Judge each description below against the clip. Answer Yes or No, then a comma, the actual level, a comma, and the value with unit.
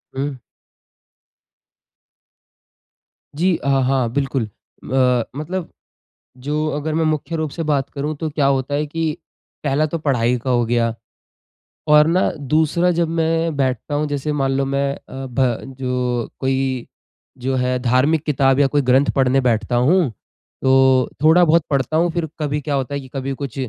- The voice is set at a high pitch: No, medium, 140 Hz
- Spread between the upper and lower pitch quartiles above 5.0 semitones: No, average, 2.9 semitones